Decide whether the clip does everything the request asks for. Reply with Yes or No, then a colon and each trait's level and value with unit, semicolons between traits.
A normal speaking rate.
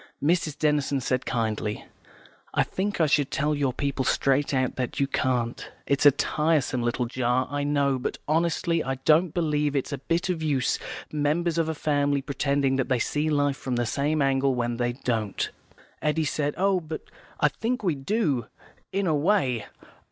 Yes: average, 180 wpm